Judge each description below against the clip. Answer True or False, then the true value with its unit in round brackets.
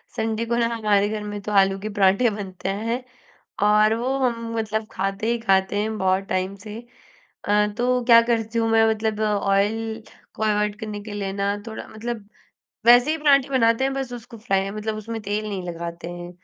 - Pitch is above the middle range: True (215 Hz)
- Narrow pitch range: True (2.3 semitones)